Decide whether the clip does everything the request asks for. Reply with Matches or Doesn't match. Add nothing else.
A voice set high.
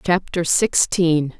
Doesn't match